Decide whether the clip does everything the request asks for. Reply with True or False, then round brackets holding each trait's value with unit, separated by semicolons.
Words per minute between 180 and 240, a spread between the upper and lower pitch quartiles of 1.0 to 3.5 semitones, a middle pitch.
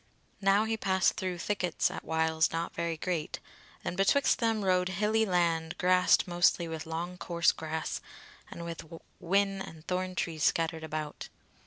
False (155 wpm; 2.8 semitones; 175 Hz)